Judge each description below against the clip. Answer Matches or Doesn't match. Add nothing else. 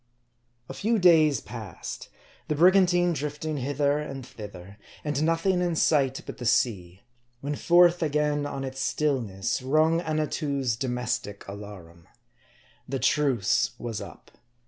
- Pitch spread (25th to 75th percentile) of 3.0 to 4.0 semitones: Doesn't match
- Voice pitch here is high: Doesn't match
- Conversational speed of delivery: Doesn't match